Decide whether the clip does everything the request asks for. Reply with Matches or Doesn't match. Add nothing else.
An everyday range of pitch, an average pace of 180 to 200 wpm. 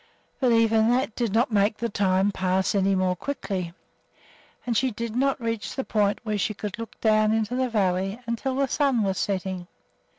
Matches